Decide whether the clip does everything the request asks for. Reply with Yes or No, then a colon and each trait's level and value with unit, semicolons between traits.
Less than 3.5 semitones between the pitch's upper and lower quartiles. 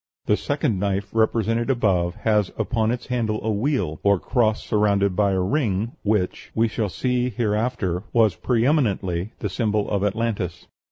Yes: average, 2.8 semitones